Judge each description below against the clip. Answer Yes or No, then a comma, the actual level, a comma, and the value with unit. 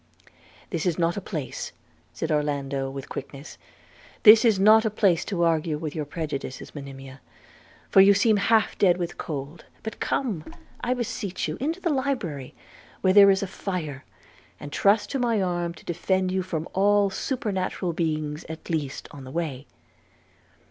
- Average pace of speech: Yes, average, 165 wpm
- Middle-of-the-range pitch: Yes, medium, 175 Hz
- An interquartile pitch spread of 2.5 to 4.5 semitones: No, wide, 5.4 semitones